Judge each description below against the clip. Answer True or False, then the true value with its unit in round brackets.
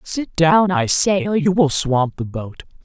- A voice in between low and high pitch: True (175 Hz)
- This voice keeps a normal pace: False (210 wpm)